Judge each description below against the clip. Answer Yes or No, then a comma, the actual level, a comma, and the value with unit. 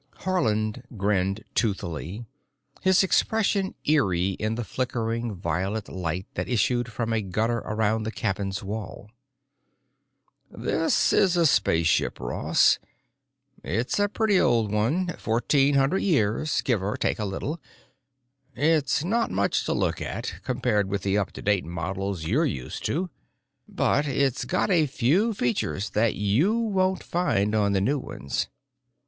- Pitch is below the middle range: Yes, low, 115 Hz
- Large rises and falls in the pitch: Yes, wide, 7.2 semitones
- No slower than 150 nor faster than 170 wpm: No, average, 140 wpm